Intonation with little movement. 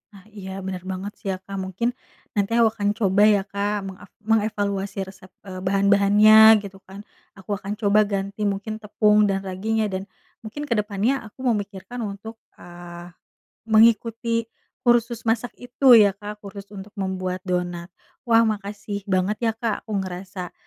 Yes: narrow, 2.1 semitones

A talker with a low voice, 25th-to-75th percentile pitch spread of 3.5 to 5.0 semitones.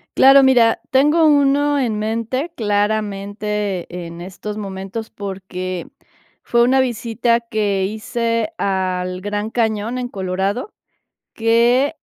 No: high, 220 Hz; average, 3.8 semitones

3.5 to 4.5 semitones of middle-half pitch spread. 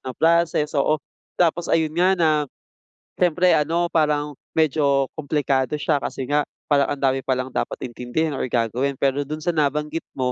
No: average, 2.9 semitones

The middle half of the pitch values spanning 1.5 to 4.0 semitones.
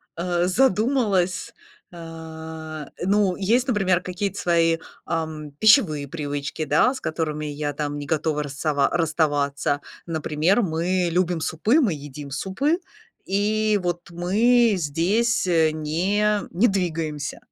No: average, 4.5 semitones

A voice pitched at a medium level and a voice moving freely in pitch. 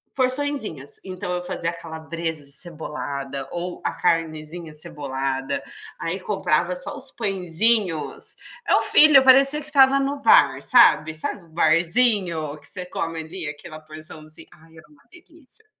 Yes: medium, 170 Hz; wide, 8.1 semitones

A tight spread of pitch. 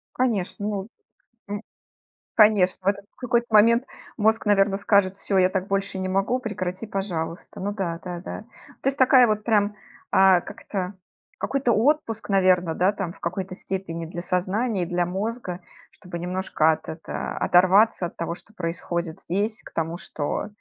No: average, 3.0 semitones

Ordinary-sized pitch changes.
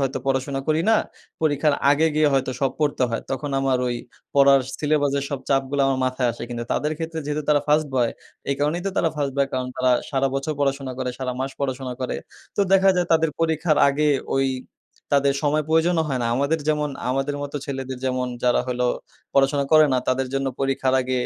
No: narrow, 2.2 semitones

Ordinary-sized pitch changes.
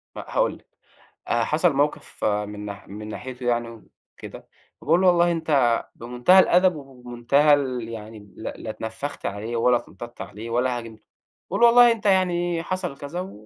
No: wide, 6.9 semitones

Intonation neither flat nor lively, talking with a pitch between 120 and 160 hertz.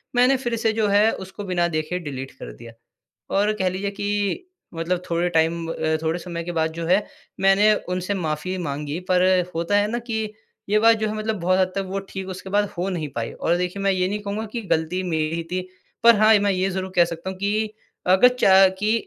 No: average, 3.3 semitones; medium, 185 Hz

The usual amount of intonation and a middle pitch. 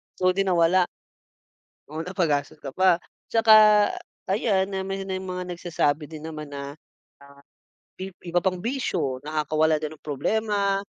Yes: average, 3.8 semitones; medium, 175 Hz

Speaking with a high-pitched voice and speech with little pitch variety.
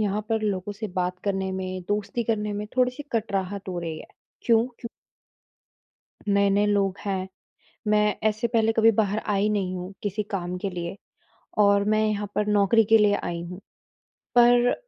Yes: high, 205 Hz; narrow, 2.1 semitones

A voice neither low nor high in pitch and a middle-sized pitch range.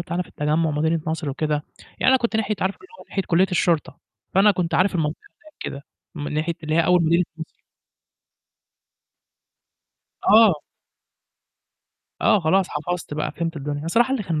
Yes: medium, 170 Hz; average, 3.6 semitones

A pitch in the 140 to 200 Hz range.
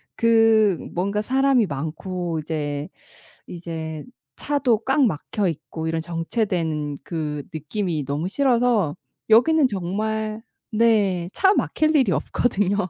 Yes: high, 190 Hz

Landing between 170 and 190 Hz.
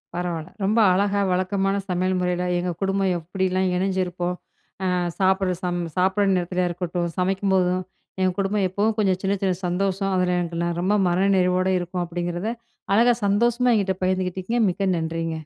Yes: medium, 185 Hz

